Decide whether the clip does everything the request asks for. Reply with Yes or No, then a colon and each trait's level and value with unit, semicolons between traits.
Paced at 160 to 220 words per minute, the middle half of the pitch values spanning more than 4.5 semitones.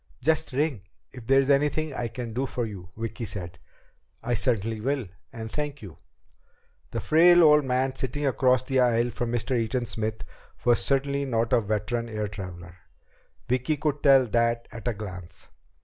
No: average, 165 wpm; average, 3.6 semitones